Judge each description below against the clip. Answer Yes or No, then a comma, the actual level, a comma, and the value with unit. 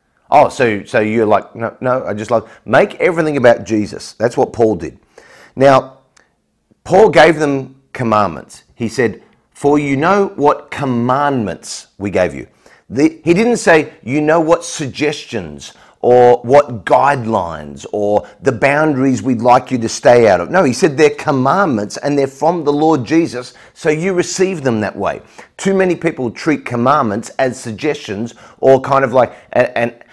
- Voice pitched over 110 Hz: Yes, low, 135 Hz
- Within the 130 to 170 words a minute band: Yes, average, 165 wpm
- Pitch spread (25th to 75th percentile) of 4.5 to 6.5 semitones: Yes, average, 4.8 semitones